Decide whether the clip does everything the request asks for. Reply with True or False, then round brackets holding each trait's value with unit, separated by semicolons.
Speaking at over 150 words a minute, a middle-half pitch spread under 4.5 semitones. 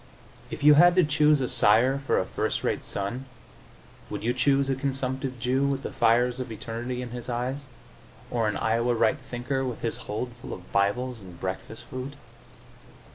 True (185 wpm; 2.8 semitones)